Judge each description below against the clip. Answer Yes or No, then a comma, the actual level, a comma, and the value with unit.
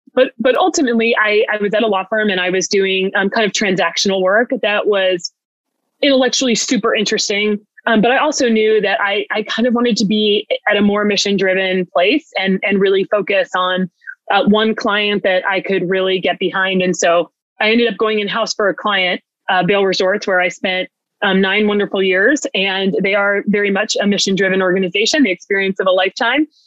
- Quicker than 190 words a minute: Yes, fast, 205 wpm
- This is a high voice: Yes, high, 205 Hz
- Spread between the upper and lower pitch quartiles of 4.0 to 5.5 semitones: No, narrow, 2.5 semitones